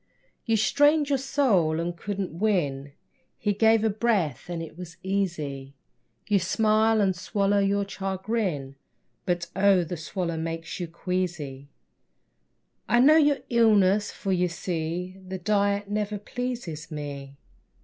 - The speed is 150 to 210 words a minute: No, slow, 135 wpm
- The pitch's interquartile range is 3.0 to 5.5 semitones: Yes, average, 4.2 semitones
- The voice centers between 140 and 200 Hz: Yes, high, 190 Hz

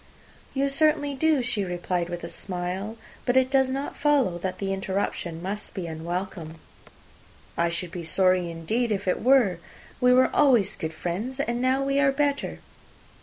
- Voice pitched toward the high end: Yes, high, 200 Hz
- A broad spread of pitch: Yes, wide, 7.0 semitones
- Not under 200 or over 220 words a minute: No, average, 170 wpm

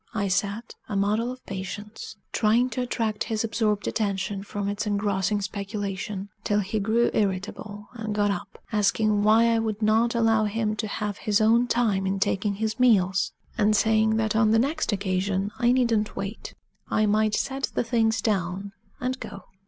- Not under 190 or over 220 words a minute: No, average, 175 wpm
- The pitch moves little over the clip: Yes, narrow, 1.9 semitones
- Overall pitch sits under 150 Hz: No, high, 210 Hz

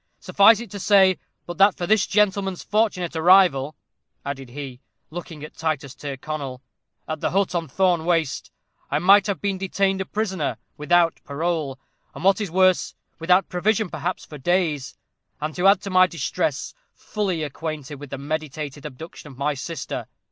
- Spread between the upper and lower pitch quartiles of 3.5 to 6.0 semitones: Yes, average, 4.5 semitones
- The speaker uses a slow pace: No, average, 165 wpm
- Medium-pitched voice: Yes, medium, 170 Hz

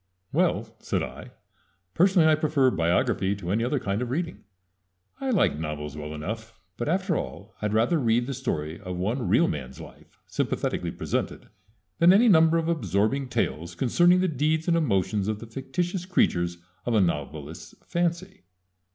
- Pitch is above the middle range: No, low, 120 Hz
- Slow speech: No, average, 165 wpm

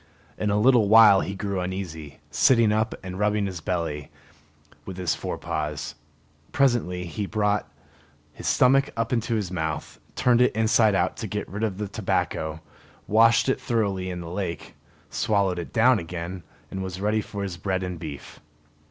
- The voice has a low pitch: Yes, low, 100 Hz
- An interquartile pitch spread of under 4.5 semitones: Yes, average, 3.5 semitones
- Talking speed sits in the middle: Yes, average, 170 wpm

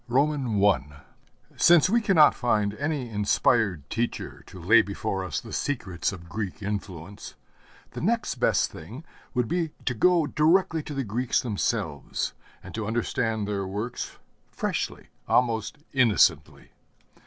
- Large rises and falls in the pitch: Yes, wide, 6.3 semitones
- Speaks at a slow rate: Yes, slow, 130 wpm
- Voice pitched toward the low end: Yes, low, 115 Hz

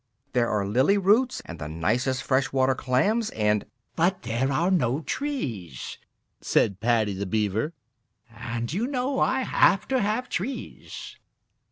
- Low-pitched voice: Yes, low, 130 Hz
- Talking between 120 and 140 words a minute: No, average, 150 wpm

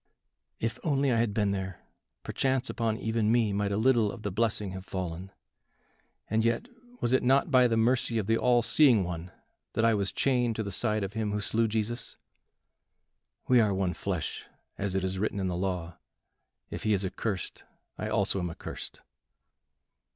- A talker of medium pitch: No, low, 110 Hz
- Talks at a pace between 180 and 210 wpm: Yes, average, 185 wpm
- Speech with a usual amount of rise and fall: Yes, average, 3.3 semitones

